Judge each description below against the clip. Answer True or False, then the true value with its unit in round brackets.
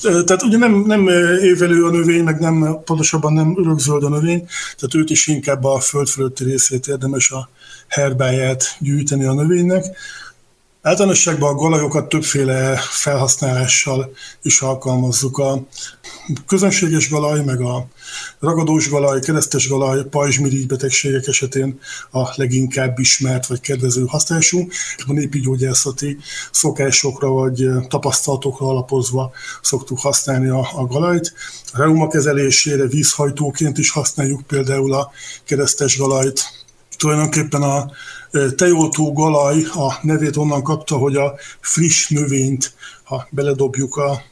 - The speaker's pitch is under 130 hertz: False (140 Hz)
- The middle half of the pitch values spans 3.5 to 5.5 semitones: False (2.6 semitones)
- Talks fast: False (120 wpm)